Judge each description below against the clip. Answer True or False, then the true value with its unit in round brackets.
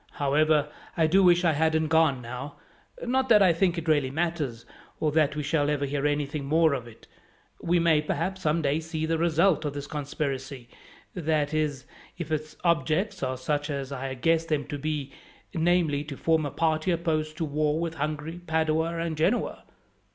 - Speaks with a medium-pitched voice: True (155 Hz)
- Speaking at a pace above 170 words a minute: True (185 wpm)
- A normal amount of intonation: False (2.3 semitones)